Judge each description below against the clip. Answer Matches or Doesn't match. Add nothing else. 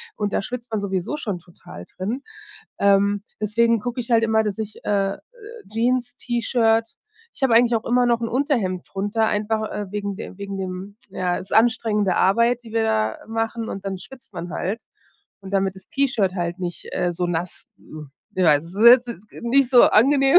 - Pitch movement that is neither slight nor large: Matches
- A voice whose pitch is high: Matches